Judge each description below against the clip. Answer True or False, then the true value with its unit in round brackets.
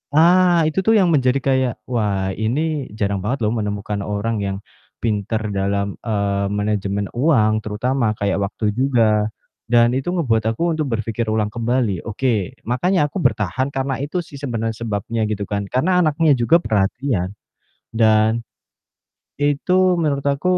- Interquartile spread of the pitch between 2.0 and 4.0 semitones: False (4.9 semitones)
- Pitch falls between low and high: False (115 Hz)